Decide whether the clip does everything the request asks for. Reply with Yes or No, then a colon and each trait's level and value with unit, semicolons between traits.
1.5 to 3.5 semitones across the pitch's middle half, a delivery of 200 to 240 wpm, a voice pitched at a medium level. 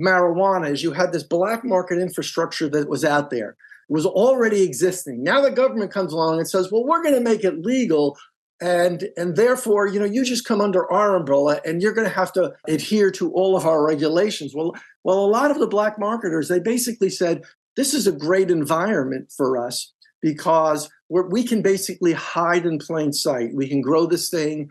No: average, 4.6 semitones; fast, 205 wpm; medium, 180 Hz